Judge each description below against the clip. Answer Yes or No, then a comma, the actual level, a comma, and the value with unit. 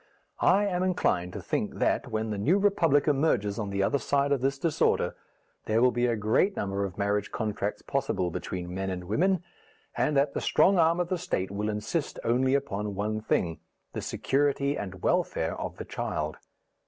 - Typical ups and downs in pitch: No, wide, 6.3 semitones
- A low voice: Yes, low, 120 Hz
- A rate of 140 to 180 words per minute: No, average, 190 wpm